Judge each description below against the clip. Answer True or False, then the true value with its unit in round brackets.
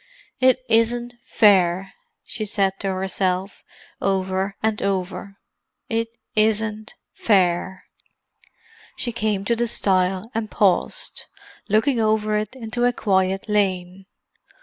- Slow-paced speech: True (110 wpm)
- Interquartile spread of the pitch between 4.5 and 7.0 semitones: False (2.8 semitones)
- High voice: True (205 Hz)